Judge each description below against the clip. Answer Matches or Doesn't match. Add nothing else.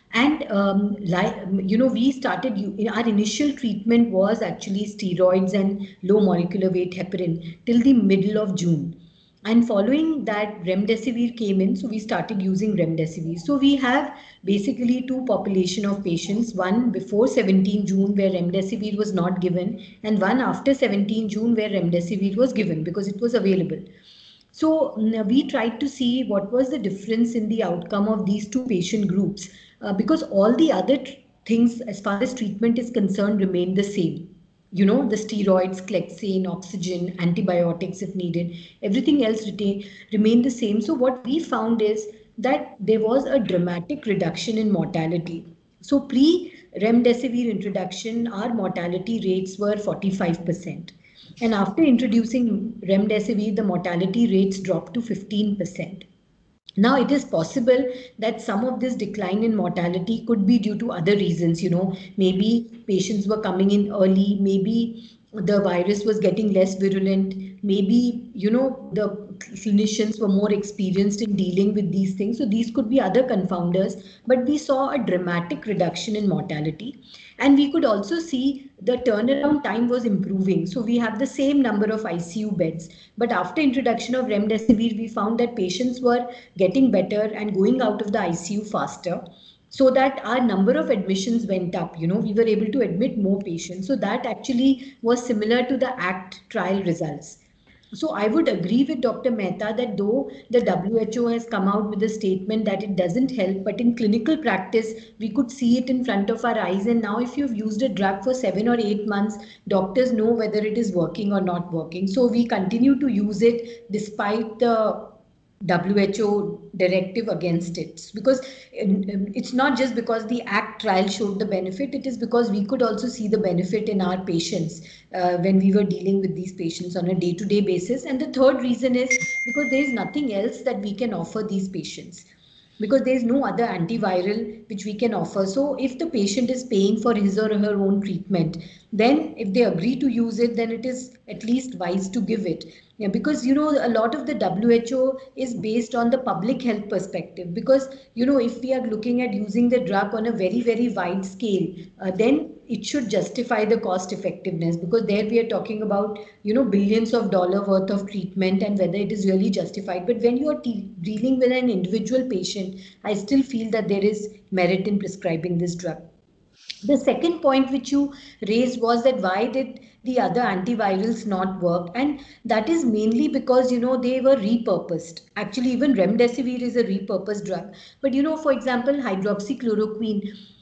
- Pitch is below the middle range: Doesn't match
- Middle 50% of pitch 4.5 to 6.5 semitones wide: Doesn't match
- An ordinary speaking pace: Matches